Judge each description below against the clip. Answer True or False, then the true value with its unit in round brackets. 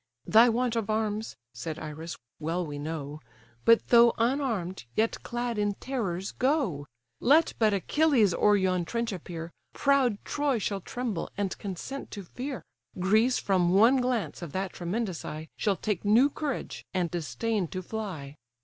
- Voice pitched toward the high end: True (205 Hz)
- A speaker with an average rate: True (155 wpm)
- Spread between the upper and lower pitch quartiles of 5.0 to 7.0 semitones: True (5.5 semitones)